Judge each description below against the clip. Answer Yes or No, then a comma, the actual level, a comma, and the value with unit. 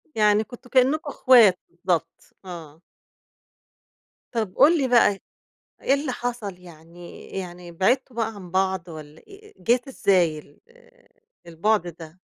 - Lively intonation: Yes, wide, 6.1 semitones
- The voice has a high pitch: Yes, high, 195 Hz